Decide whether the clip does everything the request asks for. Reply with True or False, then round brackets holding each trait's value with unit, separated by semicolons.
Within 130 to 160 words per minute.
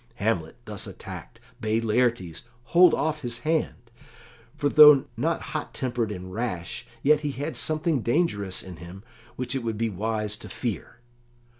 True (155 wpm)